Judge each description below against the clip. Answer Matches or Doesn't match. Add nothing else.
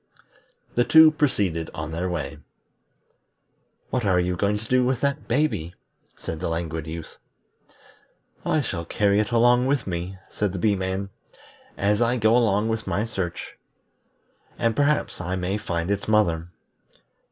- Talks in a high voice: Doesn't match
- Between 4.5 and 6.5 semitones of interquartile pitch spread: Matches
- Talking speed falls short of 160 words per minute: Matches